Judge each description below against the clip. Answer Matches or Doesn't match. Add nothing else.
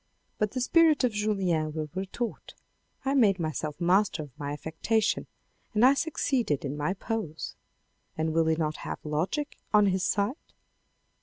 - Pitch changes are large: Matches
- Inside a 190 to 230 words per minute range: Doesn't match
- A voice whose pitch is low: Doesn't match